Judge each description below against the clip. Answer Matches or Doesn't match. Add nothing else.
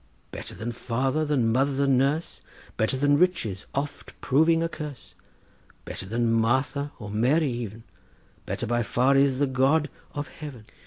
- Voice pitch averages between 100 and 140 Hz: Matches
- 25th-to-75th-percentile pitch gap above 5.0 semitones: Doesn't match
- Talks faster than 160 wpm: Doesn't match